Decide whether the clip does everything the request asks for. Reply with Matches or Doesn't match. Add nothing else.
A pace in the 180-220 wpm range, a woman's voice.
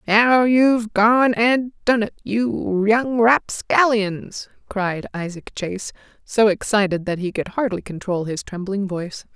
Doesn't match